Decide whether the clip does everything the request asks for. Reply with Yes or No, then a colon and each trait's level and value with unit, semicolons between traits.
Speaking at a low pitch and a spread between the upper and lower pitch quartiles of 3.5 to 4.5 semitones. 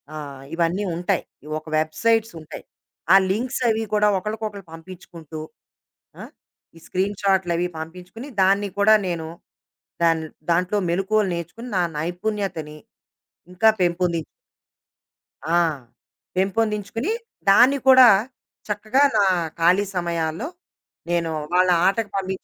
No: medium, 185 Hz; average, 3.8 semitones